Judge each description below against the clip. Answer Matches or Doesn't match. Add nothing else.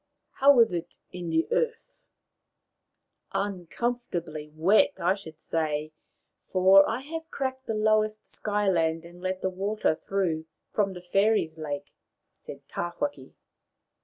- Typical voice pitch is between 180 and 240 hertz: Matches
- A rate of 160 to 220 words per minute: Doesn't match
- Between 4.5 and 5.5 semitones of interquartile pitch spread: Matches